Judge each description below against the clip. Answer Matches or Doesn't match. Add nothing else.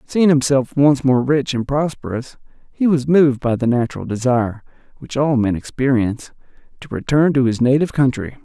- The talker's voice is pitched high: Doesn't match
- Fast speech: Doesn't match